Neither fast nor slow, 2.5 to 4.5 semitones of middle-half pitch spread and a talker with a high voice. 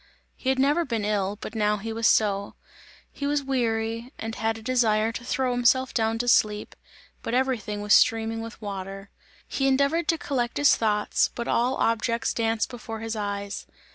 Yes: average, 180 wpm; average, 3.1 semitones; high, 225 Hz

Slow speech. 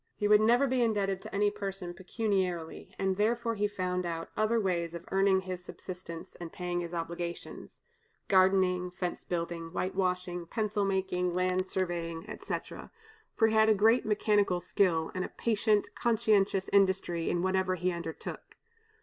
No: average, 155 wpm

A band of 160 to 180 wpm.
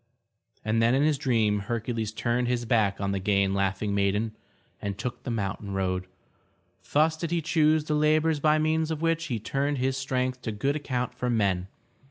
No: average, 195 wpm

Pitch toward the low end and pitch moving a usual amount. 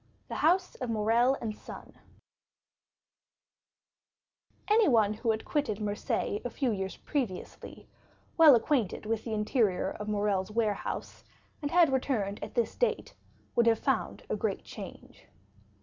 No: high, 225 Hz; average, 4.4 semitones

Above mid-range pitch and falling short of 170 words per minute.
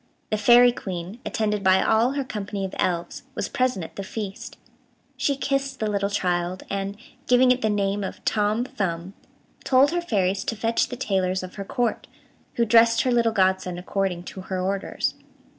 No: high, 205 Hz; average, 180 wpm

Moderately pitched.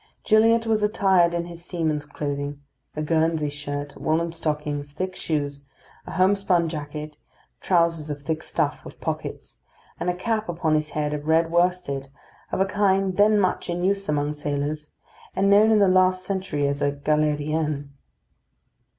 Yes: medium, 160 Hz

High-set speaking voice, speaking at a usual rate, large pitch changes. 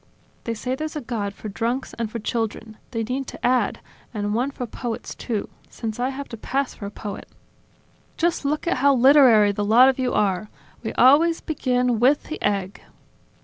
No: high, 245 Hz; average, 190 wpm; average, 3.7 semitones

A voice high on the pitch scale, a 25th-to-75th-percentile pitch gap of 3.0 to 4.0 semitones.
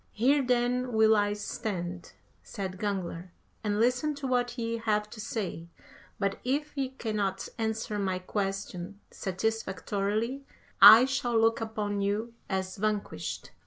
Yes: high, 215 Hz; average, 3.3 semitones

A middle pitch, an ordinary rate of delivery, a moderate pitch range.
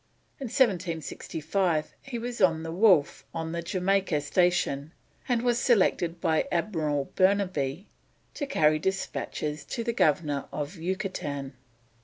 No: medium, 175 Hz; slow, 125 wpm; average, 4.5 semitones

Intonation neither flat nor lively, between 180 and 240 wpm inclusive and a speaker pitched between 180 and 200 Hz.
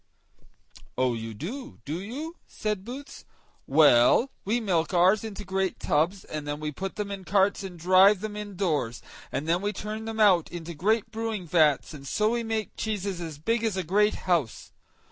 Yes: average, 4.8 semitones; average, 185 wpm; high, 190 Hz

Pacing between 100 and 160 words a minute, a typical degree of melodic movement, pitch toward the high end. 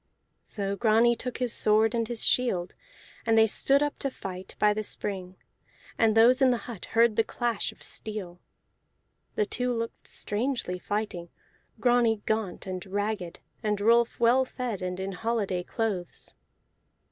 Yes: average, 155 wpm; average, 3.3 semitones; high, 220 Hz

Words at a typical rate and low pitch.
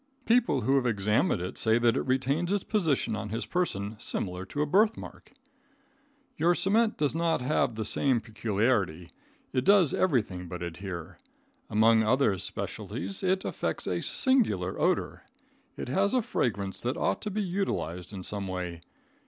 Yes: average, 160 wpm; low, 115 Hz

